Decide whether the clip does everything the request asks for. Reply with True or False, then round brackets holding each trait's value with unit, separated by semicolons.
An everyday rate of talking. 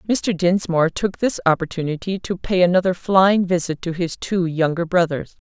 True (165 wpm)